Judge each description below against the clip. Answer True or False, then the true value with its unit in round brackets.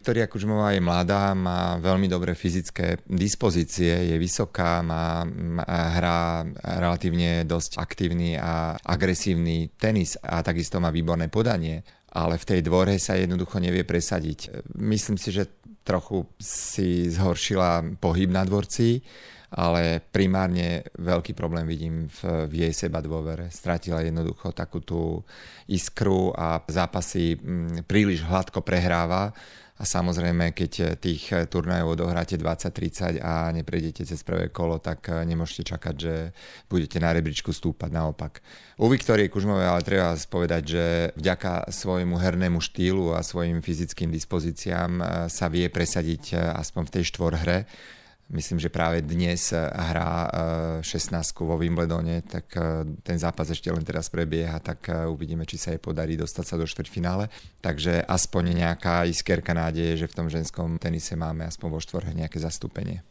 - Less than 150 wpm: True (140 wpm)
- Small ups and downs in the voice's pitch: True (1.7 semitones)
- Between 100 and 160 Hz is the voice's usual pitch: False (85 Hz)